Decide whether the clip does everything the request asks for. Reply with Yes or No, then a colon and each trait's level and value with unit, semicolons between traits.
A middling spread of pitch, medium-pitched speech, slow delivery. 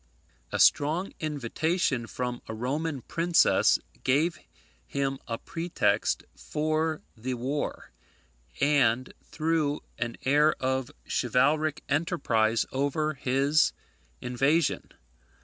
Yes: average, 3.6 semitones; medium, 145 Hz; slow, 95 wpm